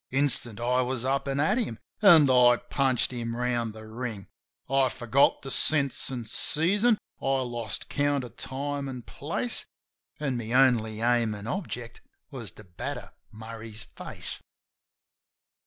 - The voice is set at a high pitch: No, low, 125 Hz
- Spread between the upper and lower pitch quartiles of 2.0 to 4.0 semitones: Yes, average, 3.2 semitones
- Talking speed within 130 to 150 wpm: Yes, average, 145 wpm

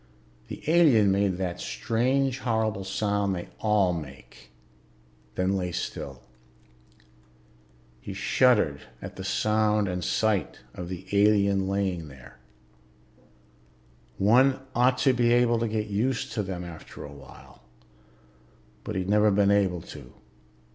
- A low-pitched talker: Yes, low, 100 Hz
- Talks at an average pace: No, slow, 125 wpm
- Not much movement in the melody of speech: No, average, 3.7 semitones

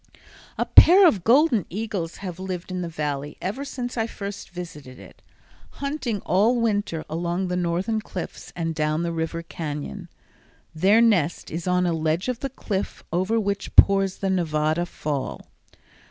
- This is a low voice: No, medium, 180 Hz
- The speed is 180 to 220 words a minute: No, average, 160 wpm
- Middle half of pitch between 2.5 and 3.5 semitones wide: No, average, 4.6 semitones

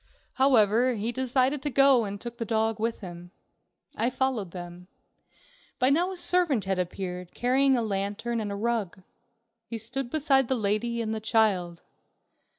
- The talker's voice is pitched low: No, high, 230 Hz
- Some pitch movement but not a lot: Yes, average, 4.4 semitones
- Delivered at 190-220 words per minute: No, average, 160 wpm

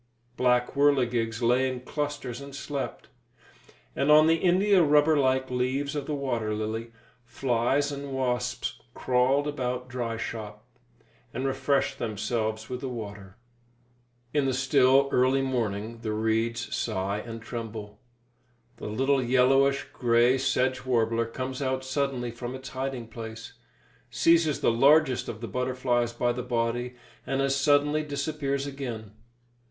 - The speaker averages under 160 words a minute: Yes, slow, 135 wpm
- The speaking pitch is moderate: No, low, 125 Hz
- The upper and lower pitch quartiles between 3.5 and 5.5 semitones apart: No, average, 2.9 semitones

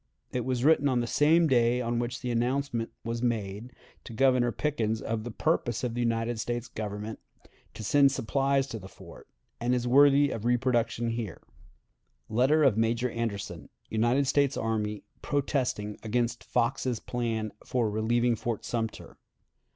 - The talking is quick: No, average, 155 wpm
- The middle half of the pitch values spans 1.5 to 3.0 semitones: Yes, narrow, 2.4 semitones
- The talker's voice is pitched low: Yes, low, 120 Hz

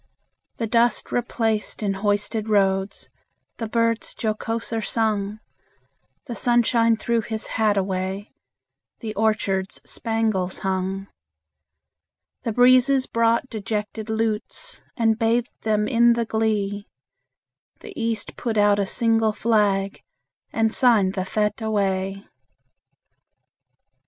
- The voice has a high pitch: Yes, high, 220 Hz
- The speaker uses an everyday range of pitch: No, narrow, 2.1 semitones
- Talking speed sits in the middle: No, slow, 105 wpm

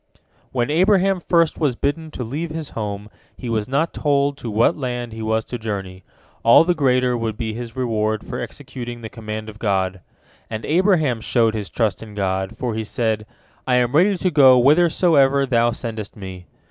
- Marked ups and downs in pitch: No, average, 4.8 semitones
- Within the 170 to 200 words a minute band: Yes, average, 185 wpm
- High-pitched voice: No, low, 120 Hz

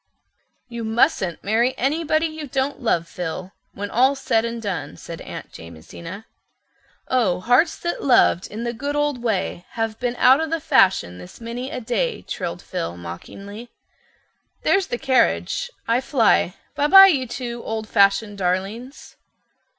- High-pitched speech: Yes, high, 235 Hz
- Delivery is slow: No, average, 150 wpm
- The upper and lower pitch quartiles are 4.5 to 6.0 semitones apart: Yes, wide, 5.4 semitones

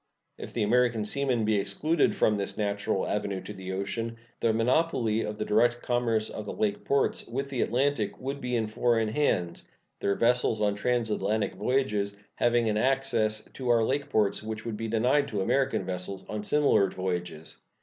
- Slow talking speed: No, average, 180 wpm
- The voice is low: Yes, low, 110 Hz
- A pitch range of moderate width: Yes, average, 3.2 semitones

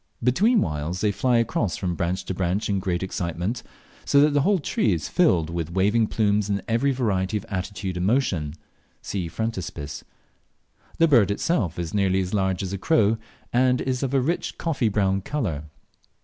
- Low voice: Yes, low, 100 Hz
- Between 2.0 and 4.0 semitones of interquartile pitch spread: No, average, 5.3 semitones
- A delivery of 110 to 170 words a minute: No, average, 180 wpm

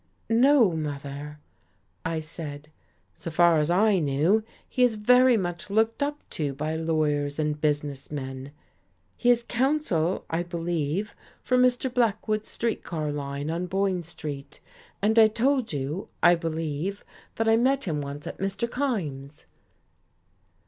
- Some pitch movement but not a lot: No, wide, 6.9 semitones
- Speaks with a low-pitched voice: No, medium, 170 Hz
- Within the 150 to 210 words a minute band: No, average, 140 wpm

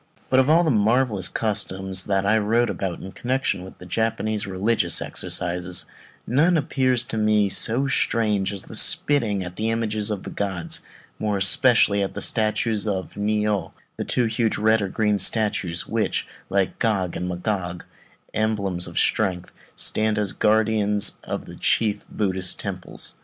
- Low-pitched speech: Yes, low, 105 Hz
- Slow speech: No, average, 170 wpm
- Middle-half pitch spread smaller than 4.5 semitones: Yes, average, 2.7 semitones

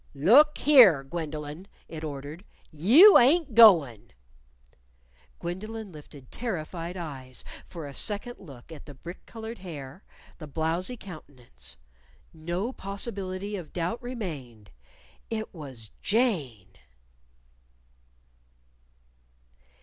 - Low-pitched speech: No, medium, 170 Hz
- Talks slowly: Yes, slow, 95 wpm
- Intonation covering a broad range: Yes, wide, 6.9 semitones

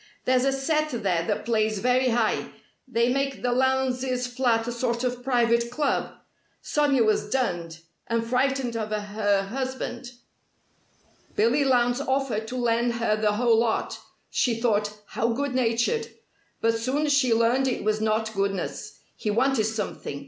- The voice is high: Yes, high, 240 Hz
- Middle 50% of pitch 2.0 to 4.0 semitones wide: Yes, average, 2.9 semitones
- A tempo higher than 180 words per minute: No, average, 150 wpm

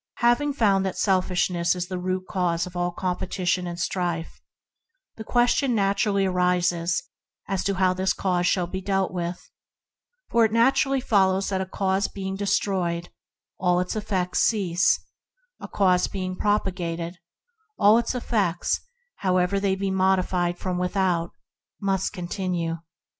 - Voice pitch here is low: No, medium, 185 Hz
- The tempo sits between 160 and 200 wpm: No, slow, 135 wpm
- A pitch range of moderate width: No, narrow, 1.8 semitones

